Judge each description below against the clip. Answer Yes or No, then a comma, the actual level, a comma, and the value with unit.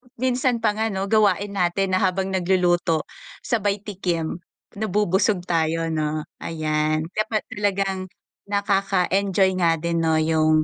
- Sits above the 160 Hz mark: Yes, high, 190 Hz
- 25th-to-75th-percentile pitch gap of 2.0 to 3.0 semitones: No, average, 3.5 semitones